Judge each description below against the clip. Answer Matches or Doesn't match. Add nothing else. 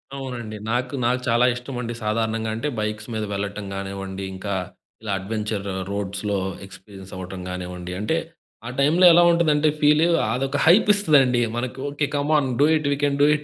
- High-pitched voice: Doesn't match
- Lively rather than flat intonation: Matches